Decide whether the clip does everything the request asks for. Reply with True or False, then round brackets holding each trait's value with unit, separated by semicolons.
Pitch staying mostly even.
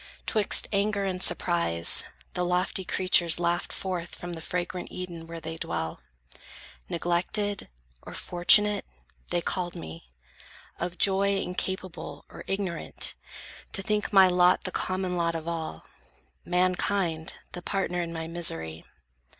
True (2.2 semitones)